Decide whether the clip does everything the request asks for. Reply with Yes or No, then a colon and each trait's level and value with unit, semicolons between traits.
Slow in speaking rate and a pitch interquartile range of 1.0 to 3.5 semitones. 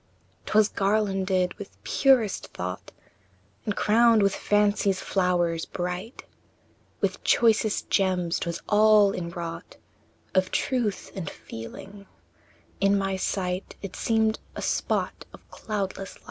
Yes: slow, 120 wpm; average, 2.7 semitones